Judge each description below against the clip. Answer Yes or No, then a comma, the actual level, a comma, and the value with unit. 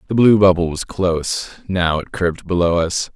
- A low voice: Yes, very low, 90 Hz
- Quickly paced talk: No, average, 190 wpm